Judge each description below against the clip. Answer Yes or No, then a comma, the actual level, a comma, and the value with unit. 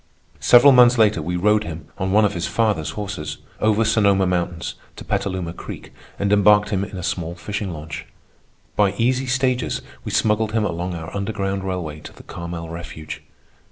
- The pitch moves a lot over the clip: No, average, 3.8 semitones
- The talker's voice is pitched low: Yes, low, 100 Hz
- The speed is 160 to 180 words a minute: Yes, average, 175 wpm